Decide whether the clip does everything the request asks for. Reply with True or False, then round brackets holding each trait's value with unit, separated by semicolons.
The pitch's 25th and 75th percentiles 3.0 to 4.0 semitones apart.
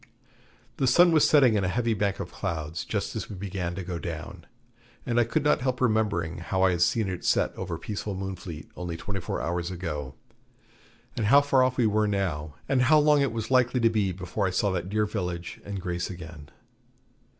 False (5.2 semitones)